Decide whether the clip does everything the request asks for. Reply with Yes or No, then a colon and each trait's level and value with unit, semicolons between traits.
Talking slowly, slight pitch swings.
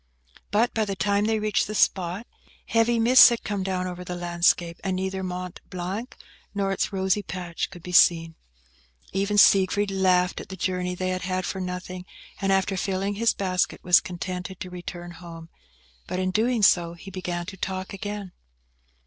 No: average, 180 wpm; narrow, 1.9 semitones